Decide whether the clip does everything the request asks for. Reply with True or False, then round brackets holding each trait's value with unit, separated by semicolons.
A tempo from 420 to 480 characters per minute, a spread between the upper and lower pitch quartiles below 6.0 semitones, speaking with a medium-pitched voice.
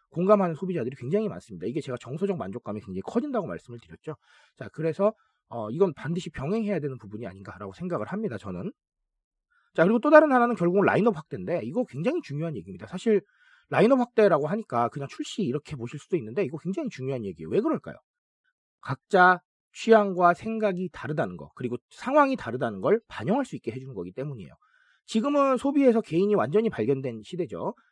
False (445 characters per minute; 8.2 semitones; 180 Hz)